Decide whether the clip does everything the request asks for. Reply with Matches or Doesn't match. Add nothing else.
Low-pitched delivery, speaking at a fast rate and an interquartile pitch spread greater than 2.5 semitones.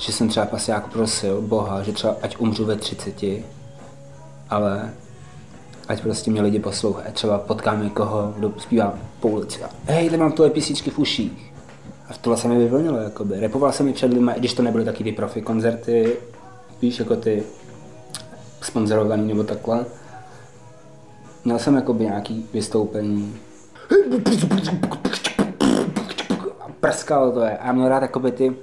Doesn't match